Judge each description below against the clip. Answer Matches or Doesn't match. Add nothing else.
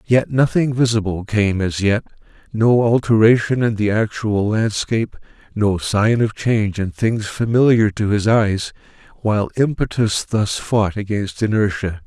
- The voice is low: Matches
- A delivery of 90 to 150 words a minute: Matches